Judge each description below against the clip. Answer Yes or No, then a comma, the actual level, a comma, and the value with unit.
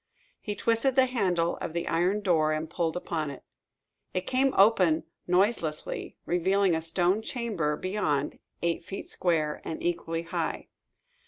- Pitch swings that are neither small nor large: Yes, average, 3.7 semitones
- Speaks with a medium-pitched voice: Yes, medium, 175 Hz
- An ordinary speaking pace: Yes, average, 145 wpm